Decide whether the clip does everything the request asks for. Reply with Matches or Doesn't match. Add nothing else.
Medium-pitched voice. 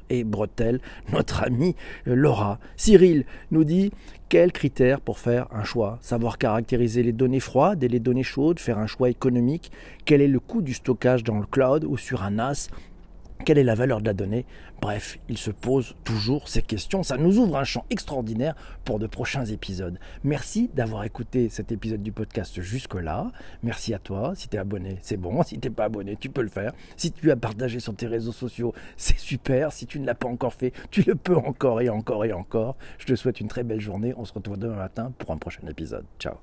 Doesn't match